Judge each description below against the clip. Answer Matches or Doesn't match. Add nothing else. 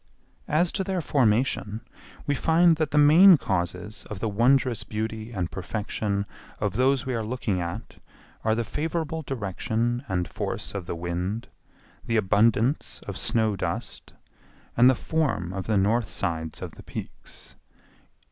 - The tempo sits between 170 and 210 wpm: Doesn't match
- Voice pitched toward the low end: Matches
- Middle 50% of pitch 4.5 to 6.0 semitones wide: Matches